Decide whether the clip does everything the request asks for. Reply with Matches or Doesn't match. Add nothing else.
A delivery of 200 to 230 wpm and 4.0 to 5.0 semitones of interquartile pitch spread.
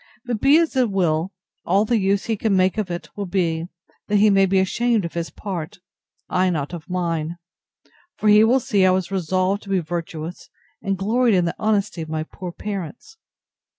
Doesn't match